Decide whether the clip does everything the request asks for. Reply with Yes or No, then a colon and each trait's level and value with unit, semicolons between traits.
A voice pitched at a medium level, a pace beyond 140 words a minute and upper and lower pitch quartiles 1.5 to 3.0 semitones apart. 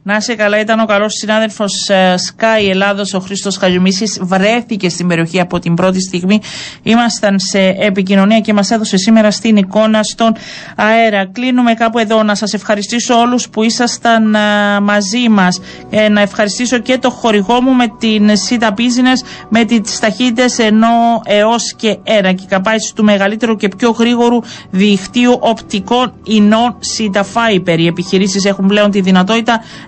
No: high, 215 Hz; average, 160 wpm; narrow, 2.6 semitones